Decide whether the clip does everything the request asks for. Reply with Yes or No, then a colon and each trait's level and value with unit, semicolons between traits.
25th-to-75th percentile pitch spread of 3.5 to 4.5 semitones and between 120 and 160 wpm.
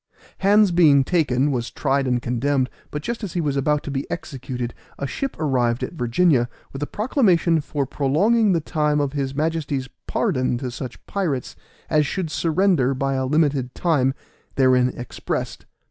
No: average, 4.1 semitones; average, 175 wpm